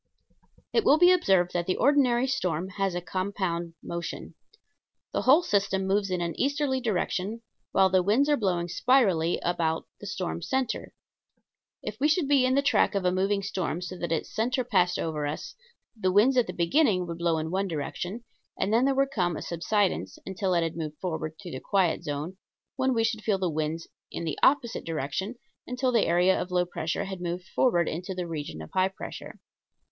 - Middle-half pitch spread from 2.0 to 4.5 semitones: No, average, 5.3 semitones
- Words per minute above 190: Yes, average, 200 wpm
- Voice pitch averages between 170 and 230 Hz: Yes, high, 190 Hz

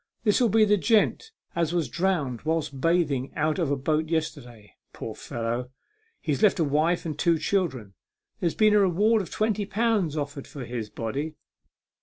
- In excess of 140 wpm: Yes, average, 170 wpm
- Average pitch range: No, wide, 5.8 semitones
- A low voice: No, medium, 160 Hz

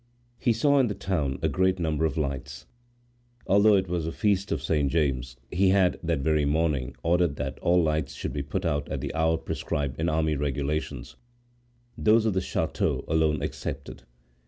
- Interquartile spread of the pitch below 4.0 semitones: No, average, 4.4 semitones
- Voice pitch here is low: Yes, very low, 80 Hz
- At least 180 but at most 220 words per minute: Yes, average, 185 wpm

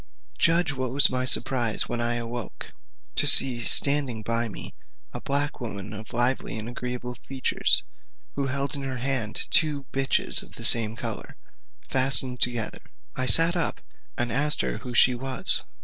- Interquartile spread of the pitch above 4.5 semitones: No, narrow, 2.5 semitones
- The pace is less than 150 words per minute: No, average, 165 wpm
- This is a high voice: No, low, 125 Hz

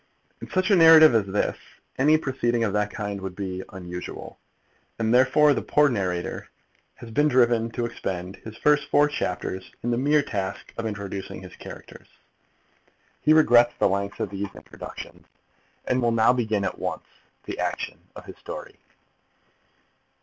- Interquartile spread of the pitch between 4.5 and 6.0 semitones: Yes, average, 5.1 semitones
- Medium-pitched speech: No, low, 115 Hz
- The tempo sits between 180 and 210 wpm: No, average, 160 wpm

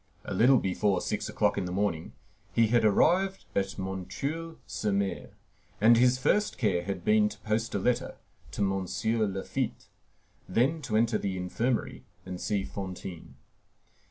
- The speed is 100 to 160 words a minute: Yes, average, 155 wpm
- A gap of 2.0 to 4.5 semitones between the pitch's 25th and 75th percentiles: Yes, average, 4.0 semitones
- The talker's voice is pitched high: No, low, 105 Hz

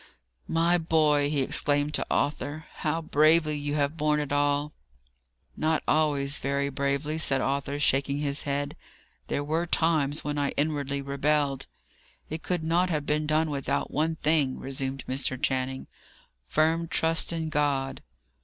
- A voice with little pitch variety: Yes, narrow, 2.0 semitones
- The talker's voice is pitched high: No, medium, 145 Hz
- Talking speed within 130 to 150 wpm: Yes, average, 145 wpm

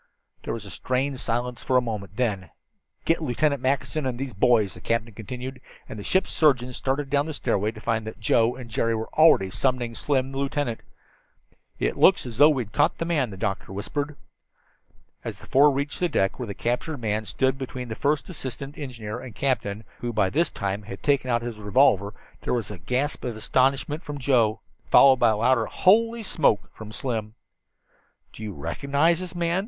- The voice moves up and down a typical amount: Yes, average, 4.3 semitones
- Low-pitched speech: Yes, low, 125 Hz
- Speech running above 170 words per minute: Yes, average, 200 wpm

